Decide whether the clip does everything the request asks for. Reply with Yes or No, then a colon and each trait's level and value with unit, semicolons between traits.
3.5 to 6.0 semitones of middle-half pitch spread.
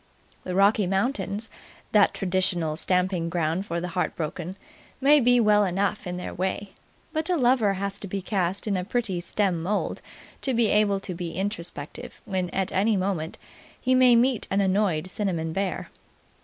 No: average, 2.9 semitones